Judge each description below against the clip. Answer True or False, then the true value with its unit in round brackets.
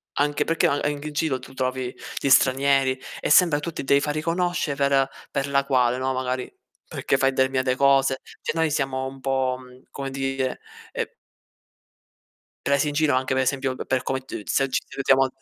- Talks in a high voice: False (135 Hz)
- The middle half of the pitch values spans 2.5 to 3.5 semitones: False (1.4 semitones)